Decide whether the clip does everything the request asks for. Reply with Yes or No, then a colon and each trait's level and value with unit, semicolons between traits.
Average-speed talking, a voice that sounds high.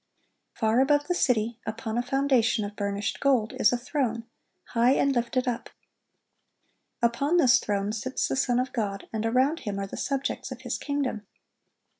Yes: average, 170 wpm; high, 240 Hz